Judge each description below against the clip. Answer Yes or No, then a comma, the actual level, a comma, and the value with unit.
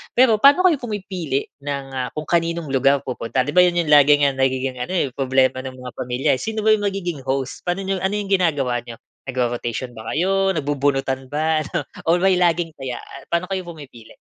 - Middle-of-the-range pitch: Yes, medium, 150 Hz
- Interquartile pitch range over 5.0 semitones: Yes, wide, 5.4 semitones